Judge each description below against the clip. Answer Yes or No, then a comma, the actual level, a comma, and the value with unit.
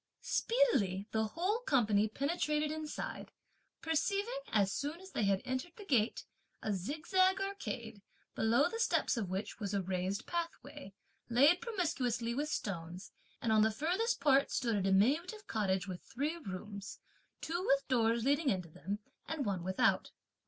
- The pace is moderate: Yes, average, 150 wpm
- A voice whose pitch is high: Yes, very high, 250 Hz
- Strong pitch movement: Yes, wide, 8.6 semitones